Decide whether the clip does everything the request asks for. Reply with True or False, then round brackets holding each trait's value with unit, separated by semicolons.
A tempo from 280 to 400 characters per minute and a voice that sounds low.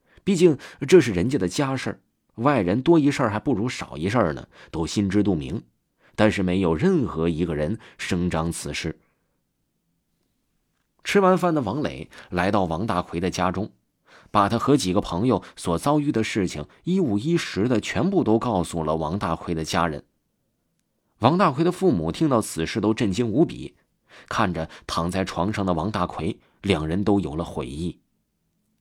False (240 characters per minute; 100 Hz)